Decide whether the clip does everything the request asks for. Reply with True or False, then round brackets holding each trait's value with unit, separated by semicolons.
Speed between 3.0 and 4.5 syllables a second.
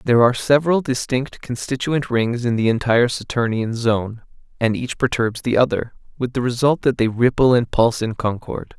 False (5.3 syllables/s)